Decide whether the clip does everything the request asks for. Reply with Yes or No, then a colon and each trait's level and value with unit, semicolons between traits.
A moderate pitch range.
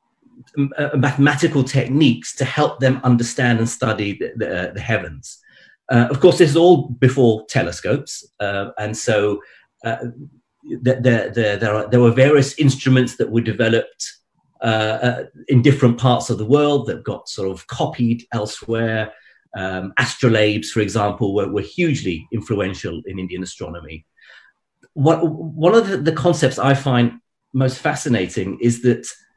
Yes: average, 4.2 semitones